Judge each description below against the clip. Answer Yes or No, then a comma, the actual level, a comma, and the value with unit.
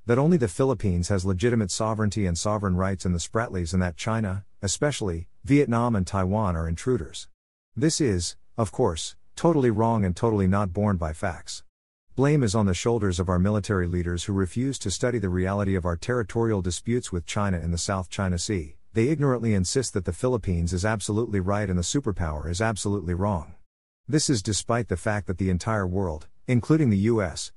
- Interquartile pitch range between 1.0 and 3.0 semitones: No, average, 4.1 semitones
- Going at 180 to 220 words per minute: Yes, average, 190 wpm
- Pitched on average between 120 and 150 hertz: No, low, 100 Hz